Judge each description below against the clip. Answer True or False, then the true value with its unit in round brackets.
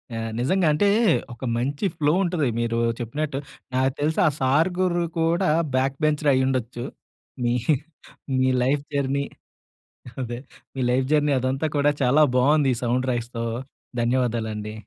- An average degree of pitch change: True (3.4 semitones)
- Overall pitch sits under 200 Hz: True (135 Hz)